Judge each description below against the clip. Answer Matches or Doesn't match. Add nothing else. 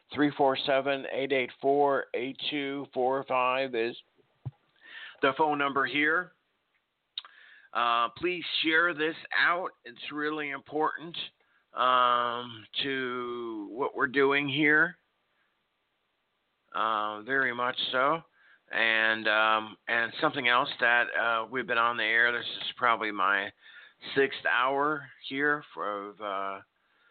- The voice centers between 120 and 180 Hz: Matches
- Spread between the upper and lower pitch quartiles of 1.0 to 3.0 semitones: Doesn't match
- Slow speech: Matches